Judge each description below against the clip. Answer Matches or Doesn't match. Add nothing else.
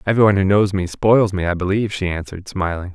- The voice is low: Matches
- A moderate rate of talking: Doesn't match